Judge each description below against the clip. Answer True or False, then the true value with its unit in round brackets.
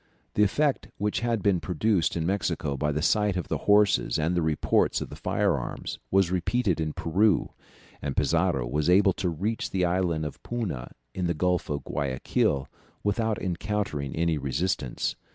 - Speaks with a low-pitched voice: True (90 Hz)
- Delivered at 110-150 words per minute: False (170 wpm)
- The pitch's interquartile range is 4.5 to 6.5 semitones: True (5.0 semitones)